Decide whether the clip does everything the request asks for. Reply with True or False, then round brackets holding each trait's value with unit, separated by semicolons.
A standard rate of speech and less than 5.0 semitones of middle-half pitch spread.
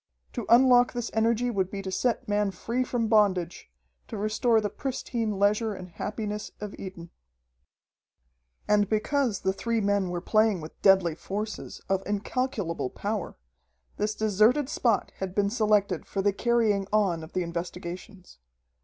True (150 wpm; 2.9 semitones)